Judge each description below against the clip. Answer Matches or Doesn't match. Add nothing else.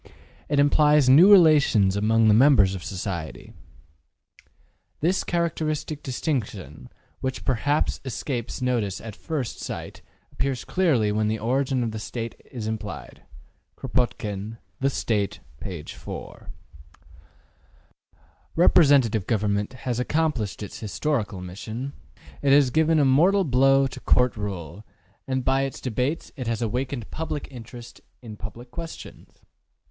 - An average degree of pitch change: Matches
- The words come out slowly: Matches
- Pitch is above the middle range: Doesn't match